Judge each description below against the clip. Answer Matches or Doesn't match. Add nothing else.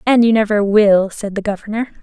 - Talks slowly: Doesn't match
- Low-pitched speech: Doesn't match